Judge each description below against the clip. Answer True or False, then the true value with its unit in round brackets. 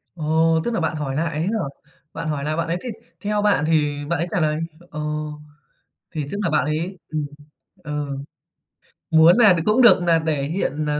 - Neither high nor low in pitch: True (160 Hz)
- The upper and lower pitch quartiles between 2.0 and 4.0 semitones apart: True (2.7 semitones)